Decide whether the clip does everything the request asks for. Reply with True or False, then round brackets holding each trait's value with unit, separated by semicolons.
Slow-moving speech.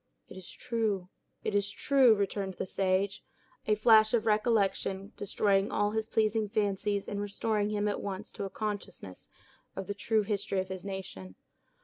False (160 wpm)